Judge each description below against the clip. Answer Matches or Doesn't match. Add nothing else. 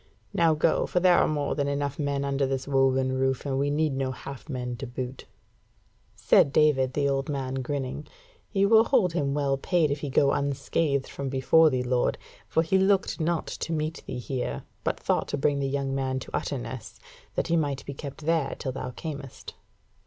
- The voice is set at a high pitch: Doesn't match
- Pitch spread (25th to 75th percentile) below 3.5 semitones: Matches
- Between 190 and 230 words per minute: Matches